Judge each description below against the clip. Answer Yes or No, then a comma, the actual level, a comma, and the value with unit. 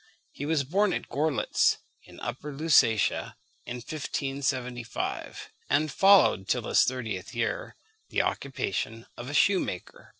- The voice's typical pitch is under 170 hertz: Yes, low, 135 Hz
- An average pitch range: Yes, average, 4.4 semitones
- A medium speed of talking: No, slow, 125 wpm